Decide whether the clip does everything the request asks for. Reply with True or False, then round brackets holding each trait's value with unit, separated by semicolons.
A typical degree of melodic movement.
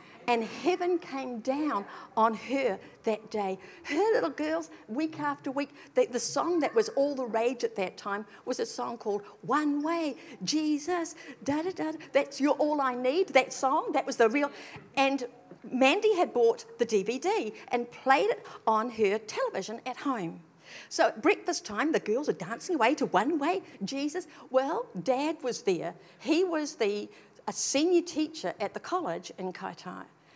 False (5.8 semitones)